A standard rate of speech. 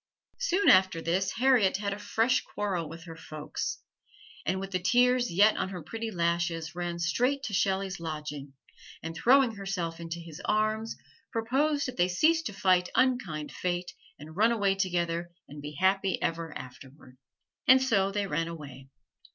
Yes: average, 165 wpm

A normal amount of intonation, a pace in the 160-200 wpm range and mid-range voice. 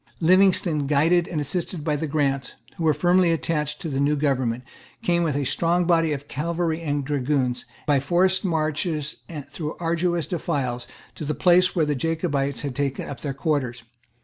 Yes: average, 3.2 semitones; average, 175 wpm; medium, 150 Hz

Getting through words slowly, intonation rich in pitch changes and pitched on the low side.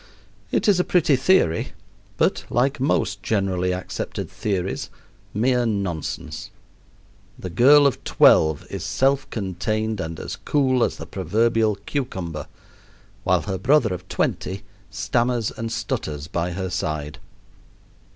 Yes: slow, 125 wpm; wide, 5.7 semitones; low, 105 Hz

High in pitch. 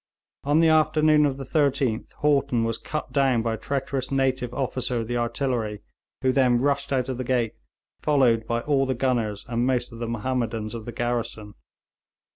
No: low, 125 Hz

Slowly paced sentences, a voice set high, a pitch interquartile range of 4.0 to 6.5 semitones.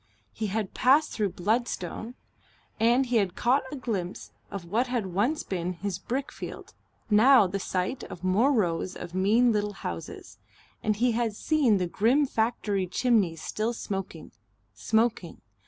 No: average, 150 wpm; high, 215 Hz; average, 4.5 semitones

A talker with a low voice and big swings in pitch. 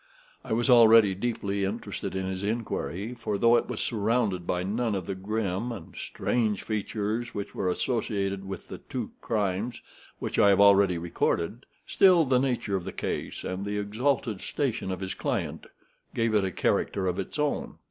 No: low, 105 Hz; average, 3.4 semitones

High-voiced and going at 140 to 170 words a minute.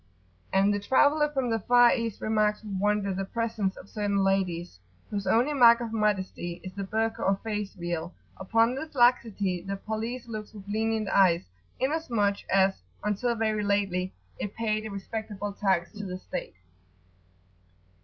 Yes: high, 210 Hz; average, 160 wpm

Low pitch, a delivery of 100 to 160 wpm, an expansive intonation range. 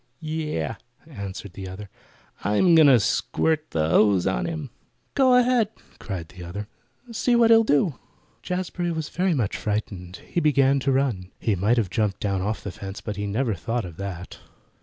No: low, 115 Hz; average, 180 wpm; wide, 8.5 semitones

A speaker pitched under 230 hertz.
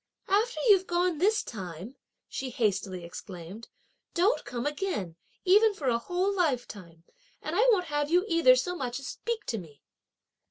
No: very high, 290 Hz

